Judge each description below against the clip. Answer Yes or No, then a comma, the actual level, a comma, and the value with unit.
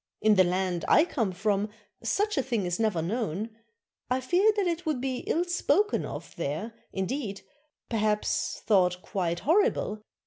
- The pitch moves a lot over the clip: Yes, wide, 7.2 semitones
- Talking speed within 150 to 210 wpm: Yes, average, 165 wpm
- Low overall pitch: No, high, 215 Hz